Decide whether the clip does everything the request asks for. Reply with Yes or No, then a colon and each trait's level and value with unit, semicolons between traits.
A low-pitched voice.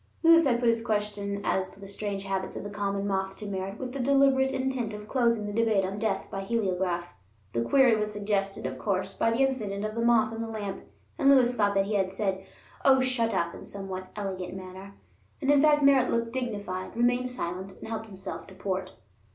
No: high, 210 Hz